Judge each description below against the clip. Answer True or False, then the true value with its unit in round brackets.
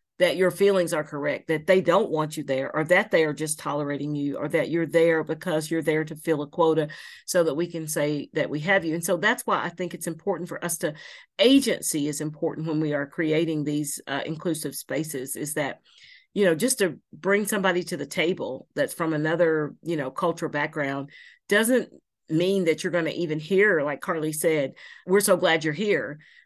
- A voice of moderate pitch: True (160 Hz)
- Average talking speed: False (215 wpm)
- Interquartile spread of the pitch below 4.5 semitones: True (2.9 semitones)